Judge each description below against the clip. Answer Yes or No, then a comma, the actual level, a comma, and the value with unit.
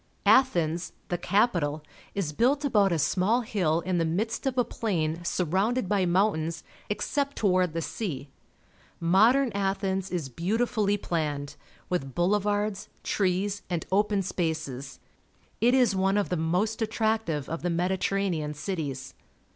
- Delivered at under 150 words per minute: Yes, average, 140 wpm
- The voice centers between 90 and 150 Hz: No, high, 190 Hz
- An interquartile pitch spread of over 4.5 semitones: No, average, 4.2 semitones